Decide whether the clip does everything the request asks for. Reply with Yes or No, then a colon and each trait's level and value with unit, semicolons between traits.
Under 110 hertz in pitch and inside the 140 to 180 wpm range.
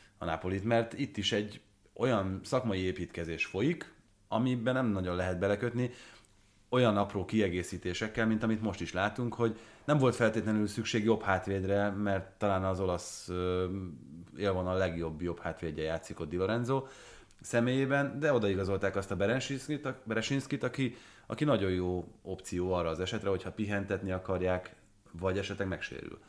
Yes: low, 100 Hz; average, 150 wpm